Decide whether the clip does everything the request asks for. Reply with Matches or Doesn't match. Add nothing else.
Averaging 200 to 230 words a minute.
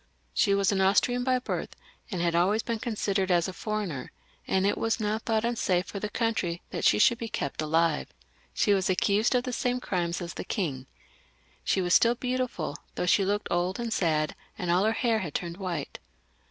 Matches